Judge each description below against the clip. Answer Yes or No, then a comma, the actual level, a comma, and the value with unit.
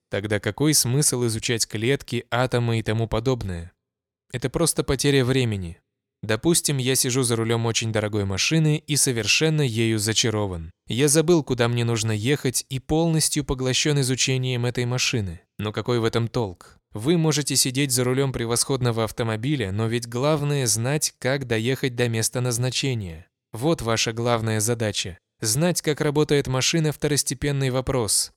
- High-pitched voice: No, low, 125 Hz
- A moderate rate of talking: Yes, average, 145 wpm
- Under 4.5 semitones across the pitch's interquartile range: Yes, average, 4.1 semitones